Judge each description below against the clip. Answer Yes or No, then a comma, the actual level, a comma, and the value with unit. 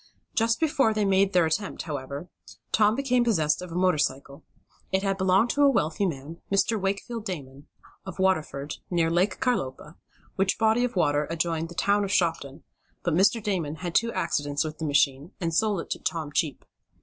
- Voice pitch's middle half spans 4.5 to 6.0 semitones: Yes, average, 5.0 semitones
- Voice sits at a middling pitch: Yes, medium, 180 Hz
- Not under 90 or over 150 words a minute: No, average, 185 wpm